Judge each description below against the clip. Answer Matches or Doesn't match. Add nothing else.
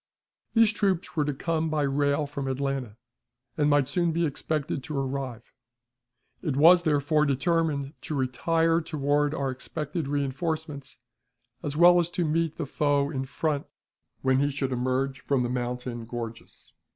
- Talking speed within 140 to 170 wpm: Matches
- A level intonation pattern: Doesn't match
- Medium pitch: Matches